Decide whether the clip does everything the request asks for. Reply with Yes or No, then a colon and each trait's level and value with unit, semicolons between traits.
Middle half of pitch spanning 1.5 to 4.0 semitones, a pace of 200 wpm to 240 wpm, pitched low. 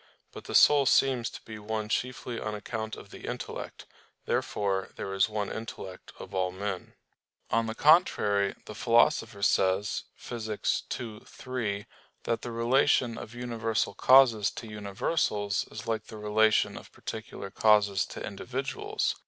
No: narrow, 2.5 semitones; average, 145 wpm; low, 110 Hz